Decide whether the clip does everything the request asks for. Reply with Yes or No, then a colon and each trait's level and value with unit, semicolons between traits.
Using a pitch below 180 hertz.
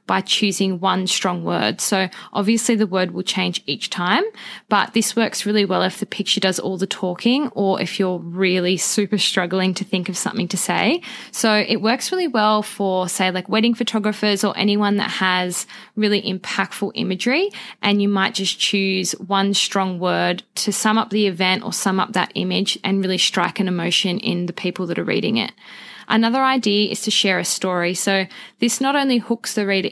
No: high, 200 Hz